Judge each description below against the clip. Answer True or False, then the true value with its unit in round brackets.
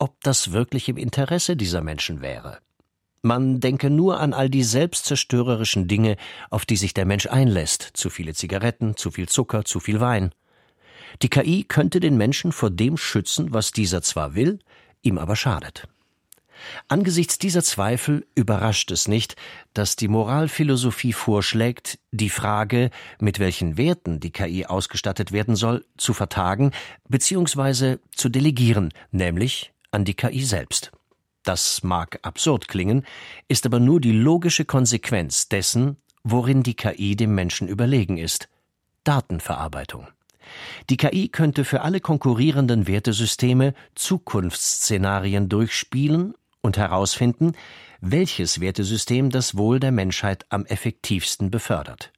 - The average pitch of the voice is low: True (115 Hz)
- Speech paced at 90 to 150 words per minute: True (130 wpm)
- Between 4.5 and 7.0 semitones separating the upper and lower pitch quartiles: True (5.1 semitones)